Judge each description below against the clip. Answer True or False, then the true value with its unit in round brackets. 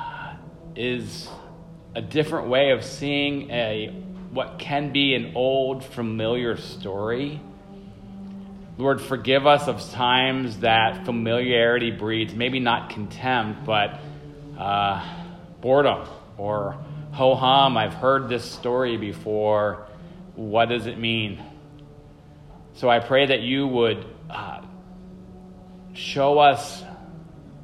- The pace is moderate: False (105 wpm)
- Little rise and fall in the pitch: False (4.6 semitones)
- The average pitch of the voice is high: False (130 Hz)